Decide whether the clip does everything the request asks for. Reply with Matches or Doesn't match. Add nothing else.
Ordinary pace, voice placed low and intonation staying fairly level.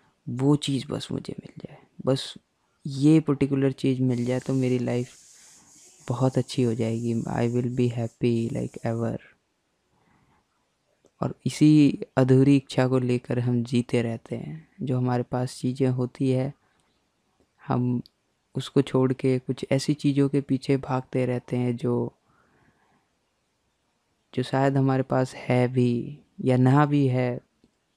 Matches